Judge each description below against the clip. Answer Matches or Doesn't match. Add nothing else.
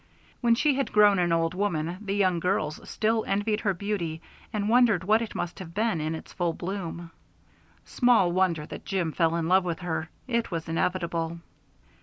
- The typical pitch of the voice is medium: Matches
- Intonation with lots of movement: Doesn't match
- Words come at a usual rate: Matches